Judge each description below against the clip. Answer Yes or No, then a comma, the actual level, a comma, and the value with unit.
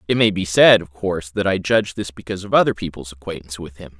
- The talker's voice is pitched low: Yes, very low, 90 Hz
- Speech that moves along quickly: Yes, fast, 255 wpm